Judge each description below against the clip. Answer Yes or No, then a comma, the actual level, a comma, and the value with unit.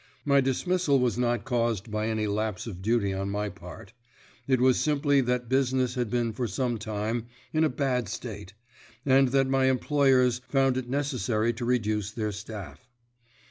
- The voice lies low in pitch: Yes, low, 120 Hz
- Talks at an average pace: Yes, average, 170 wpm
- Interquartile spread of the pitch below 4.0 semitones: Yes, average, 3.6 semitones